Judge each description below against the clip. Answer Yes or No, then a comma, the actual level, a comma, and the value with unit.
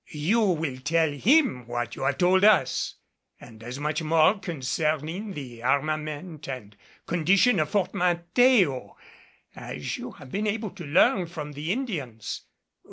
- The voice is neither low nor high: Yes, medium, 160 Hz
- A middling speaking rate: Yes, average, 145 wpm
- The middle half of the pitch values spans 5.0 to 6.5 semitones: Yes, wide, 5.6 semitones